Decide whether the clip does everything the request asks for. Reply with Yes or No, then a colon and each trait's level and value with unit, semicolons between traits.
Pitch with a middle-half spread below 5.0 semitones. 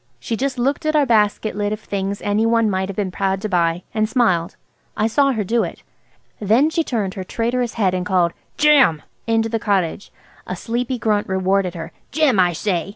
Yes: average, 4.0 semitones